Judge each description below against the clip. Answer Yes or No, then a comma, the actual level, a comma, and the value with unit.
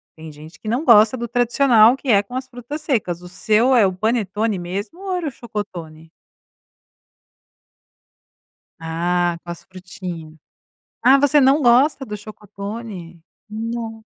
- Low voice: No, high, 215 Hz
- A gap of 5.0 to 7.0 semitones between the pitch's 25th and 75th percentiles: Yes, wide, 5.5 semitones